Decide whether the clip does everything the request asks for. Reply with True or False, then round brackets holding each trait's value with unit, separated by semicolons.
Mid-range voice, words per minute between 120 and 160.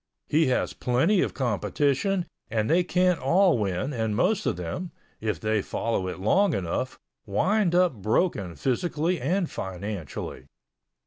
False (130 Hz; 140 wpm)